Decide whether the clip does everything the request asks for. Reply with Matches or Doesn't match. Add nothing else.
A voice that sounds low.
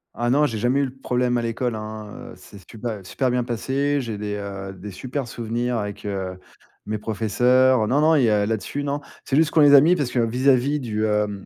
Matches